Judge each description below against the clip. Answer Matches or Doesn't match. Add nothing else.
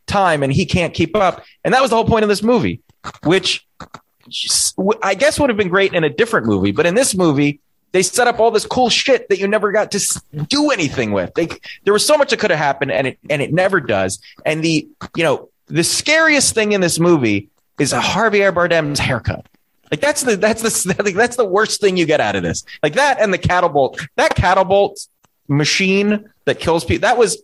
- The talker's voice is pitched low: Doesn't match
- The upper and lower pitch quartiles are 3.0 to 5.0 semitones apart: Doesn't match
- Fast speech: Matches